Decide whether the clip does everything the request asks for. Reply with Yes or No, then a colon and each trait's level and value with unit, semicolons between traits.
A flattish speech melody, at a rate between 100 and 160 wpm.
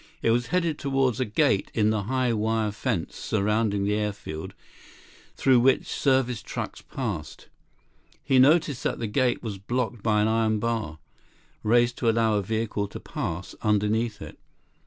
No: average, 3.0 semitones; average, 155 wpm